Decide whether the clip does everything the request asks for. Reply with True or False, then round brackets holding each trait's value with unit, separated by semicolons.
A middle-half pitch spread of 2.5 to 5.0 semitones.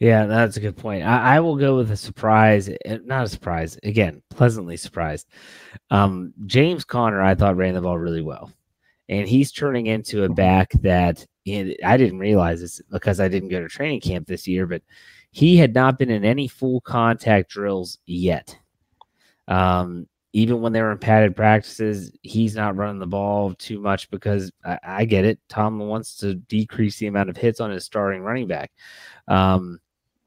True (3.1 semitones)